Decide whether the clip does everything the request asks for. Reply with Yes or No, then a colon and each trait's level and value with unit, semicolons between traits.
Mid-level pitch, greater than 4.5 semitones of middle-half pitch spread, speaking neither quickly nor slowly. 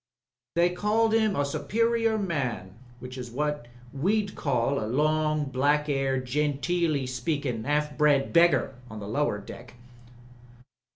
No: medium, 145 Hz; average, 5.0 semitones; slow, 130 wpm